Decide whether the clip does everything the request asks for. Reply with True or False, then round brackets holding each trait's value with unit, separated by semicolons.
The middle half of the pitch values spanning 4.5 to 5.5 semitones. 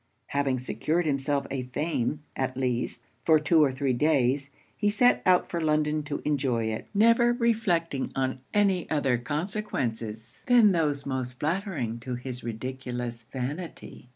True (5.1 semitones)